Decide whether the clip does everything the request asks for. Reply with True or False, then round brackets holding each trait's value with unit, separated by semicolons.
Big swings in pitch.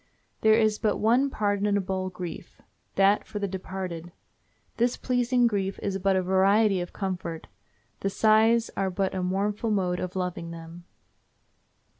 False (2.8 semitones)